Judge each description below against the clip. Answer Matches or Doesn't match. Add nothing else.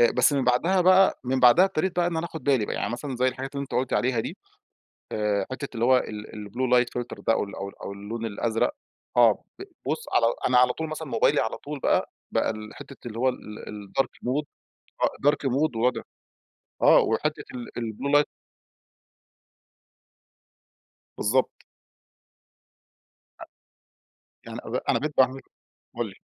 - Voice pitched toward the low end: Matches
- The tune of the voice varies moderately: Matches